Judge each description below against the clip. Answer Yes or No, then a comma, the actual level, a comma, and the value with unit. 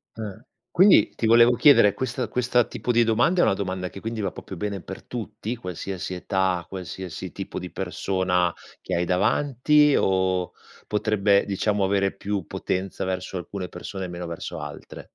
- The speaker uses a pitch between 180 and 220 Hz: No, low, 100 Hz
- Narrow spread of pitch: No, average, 3.5 semitones